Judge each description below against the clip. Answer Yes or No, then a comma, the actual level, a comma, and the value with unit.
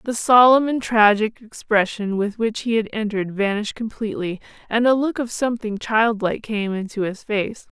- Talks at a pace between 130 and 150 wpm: No, average, 170 wpm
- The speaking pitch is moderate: No, high, 220 Hz